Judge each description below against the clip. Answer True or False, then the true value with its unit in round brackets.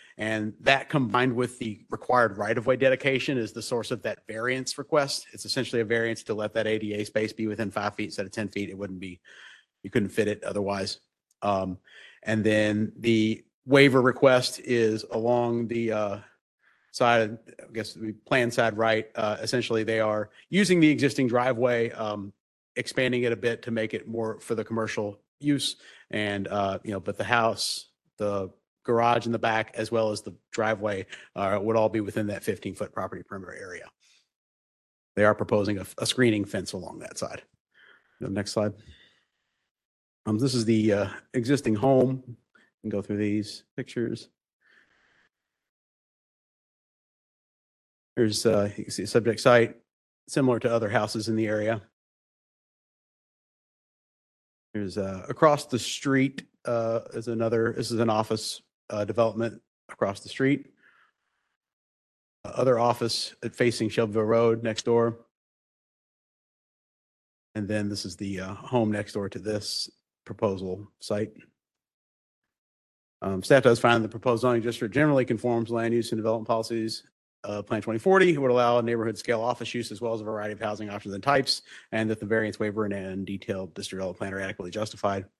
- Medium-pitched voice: False (110 Hz)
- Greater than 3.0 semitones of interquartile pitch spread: False (2.4 semitones)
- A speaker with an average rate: True (165 wpm)